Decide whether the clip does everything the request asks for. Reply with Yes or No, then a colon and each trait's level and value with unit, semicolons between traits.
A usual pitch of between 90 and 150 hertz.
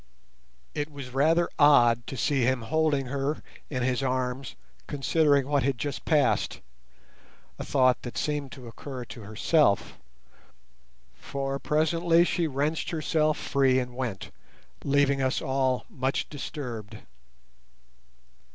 Yes: low, 135 Hz